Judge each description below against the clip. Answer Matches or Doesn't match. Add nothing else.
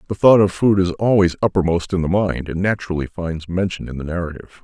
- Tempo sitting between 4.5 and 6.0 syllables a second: Doesn't match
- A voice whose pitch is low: Matches